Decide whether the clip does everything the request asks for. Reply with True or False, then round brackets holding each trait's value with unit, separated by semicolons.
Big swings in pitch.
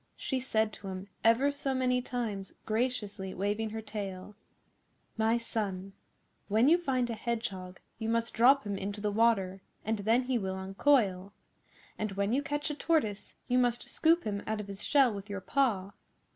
False (4.0 semitones)